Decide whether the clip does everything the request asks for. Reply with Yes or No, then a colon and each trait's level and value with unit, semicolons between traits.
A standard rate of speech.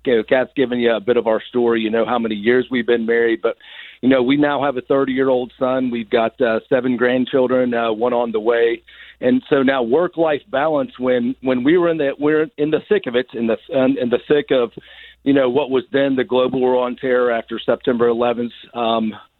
No: fast, 230 wpm